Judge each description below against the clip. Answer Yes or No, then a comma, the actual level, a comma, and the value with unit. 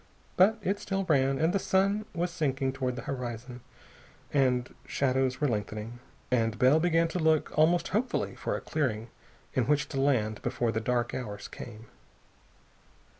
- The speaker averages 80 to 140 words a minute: No, average, 160 wpm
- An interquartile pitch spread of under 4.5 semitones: No, average, 5.3 semitones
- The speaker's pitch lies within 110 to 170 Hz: Yes, low, 135 Hz